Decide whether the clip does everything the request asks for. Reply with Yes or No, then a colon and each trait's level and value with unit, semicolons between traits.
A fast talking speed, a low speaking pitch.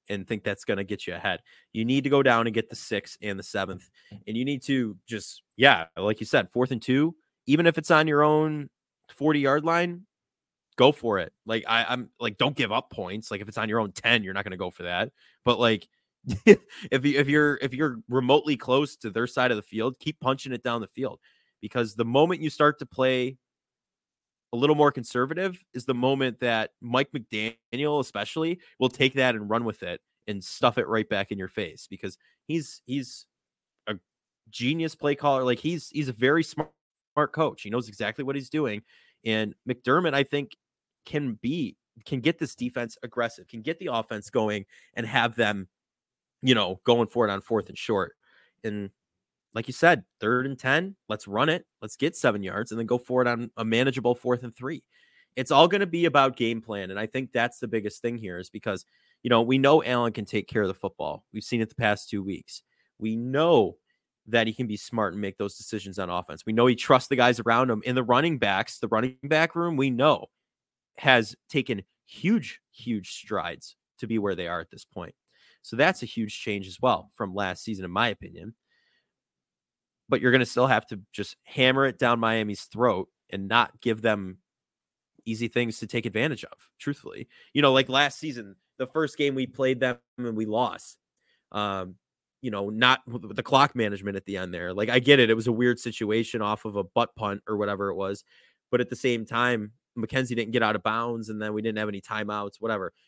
Yes: fast, 215 wpm; low, 120 Hz